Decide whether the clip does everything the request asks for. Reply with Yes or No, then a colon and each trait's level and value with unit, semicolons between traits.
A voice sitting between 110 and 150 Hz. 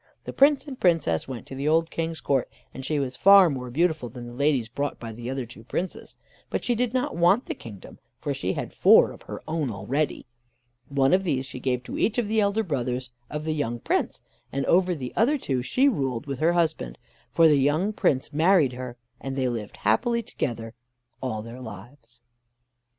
Yes: medium, 140 Hz